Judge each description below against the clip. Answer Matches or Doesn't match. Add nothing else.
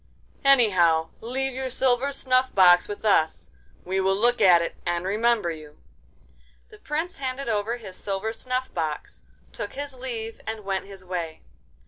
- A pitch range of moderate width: Doesn't match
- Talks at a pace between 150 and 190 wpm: Matches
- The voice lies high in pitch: Matches